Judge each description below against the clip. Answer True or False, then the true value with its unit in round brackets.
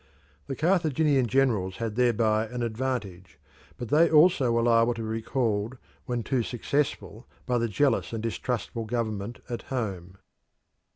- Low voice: True (115 Hz)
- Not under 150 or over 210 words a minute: False (140 wpm)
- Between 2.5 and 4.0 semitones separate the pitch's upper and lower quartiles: True (3.1 semitones)